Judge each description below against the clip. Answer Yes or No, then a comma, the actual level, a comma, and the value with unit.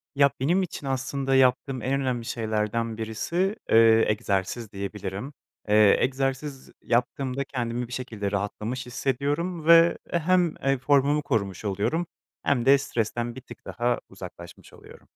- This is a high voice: No, low, 125 Hz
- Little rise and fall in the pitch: No, average, 3.9 semitones